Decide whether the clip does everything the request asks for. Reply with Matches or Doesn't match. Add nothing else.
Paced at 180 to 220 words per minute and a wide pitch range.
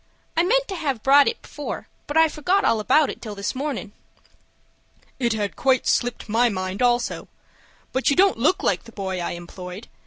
Matches